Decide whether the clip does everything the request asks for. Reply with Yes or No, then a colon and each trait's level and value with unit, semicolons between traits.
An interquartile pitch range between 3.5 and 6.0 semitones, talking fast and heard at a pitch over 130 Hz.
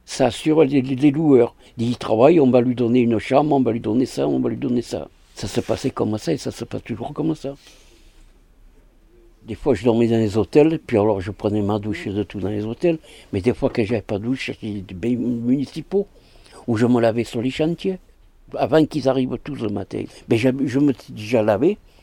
No: average, 4.0 semitones; fast, 230 wpm; low, 120 Hz